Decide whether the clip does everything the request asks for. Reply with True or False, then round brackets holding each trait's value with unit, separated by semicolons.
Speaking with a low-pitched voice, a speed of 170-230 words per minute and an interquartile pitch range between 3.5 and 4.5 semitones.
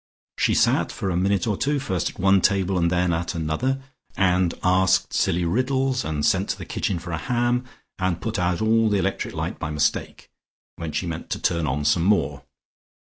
True (95 Hz; 205 wpm; 4.2 semitones)